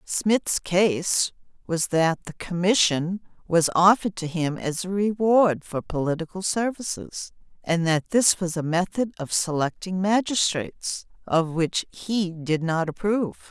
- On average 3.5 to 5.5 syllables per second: Yes, 4.1 syllables/s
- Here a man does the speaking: No, female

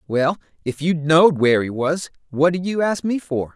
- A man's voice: Yes, male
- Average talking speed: No, fast, 220 wpm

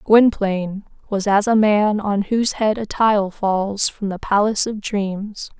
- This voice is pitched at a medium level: No, high, 205 Hz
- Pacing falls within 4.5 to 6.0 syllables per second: No, 4.1 syllables/s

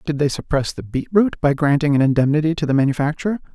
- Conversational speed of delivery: No, fast, 220 wpm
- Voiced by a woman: No, male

